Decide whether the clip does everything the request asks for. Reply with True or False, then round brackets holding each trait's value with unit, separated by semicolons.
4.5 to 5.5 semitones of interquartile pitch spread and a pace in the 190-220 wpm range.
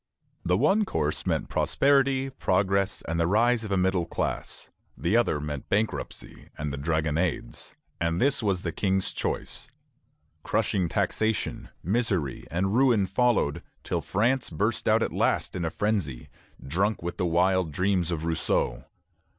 False (4.8 semitones; 150 wpm)